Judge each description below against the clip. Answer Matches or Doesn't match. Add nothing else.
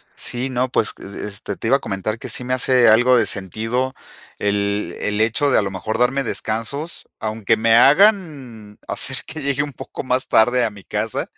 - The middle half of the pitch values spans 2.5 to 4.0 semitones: Matches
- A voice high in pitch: Doesn't match